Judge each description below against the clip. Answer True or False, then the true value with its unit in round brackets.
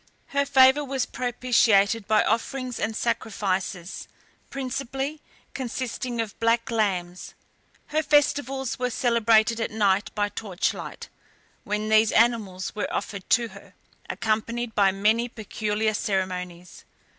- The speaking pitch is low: False (225 Hz)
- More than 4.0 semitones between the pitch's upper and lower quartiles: False (3.3 semitones)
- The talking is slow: True (115 wpm)